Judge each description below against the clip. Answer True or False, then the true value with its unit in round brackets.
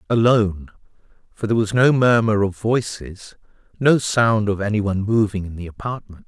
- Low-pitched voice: True (105 Hz)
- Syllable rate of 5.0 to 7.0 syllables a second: True (5.3 syllables/s)